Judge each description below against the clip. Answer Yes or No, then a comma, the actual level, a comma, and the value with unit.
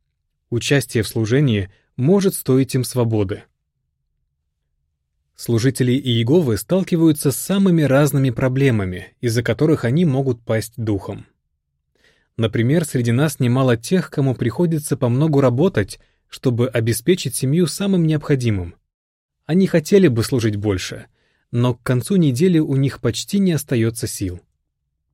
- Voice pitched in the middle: No, low, 125 Hz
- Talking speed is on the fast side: No, average, 115 wpm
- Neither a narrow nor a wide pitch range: No, wide, 5.7 semitones